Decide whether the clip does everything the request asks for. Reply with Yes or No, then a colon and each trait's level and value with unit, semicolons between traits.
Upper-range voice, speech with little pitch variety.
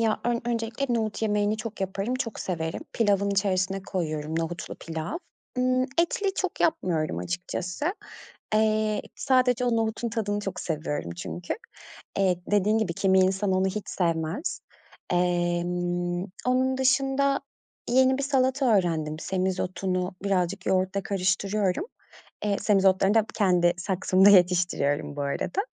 No: high, 195 Hz; average, 4.3 semitones